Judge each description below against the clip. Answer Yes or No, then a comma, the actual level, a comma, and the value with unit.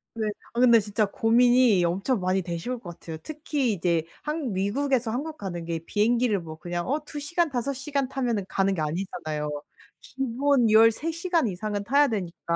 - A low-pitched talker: No, high, 225 Hz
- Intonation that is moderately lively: No, wide, 6.5 semitones